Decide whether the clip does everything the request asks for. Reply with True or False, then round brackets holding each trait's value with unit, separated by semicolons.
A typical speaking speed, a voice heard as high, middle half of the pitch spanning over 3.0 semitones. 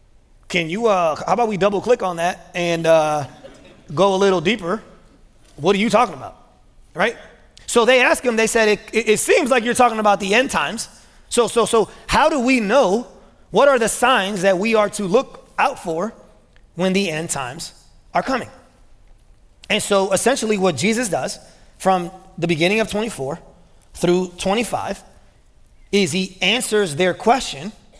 True (175 wpm; 200 Hz; 3.5 semitones)